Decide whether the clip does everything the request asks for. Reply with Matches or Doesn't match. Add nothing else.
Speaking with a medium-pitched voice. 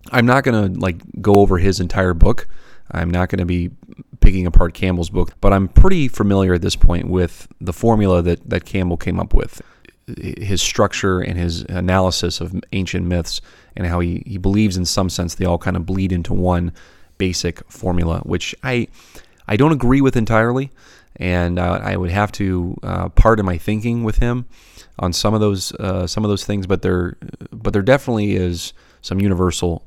Doesn't match